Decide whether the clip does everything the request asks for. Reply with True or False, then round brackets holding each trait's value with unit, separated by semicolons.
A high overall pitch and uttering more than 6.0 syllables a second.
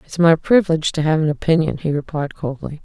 False (155 Hz; 6.5 syllables/s)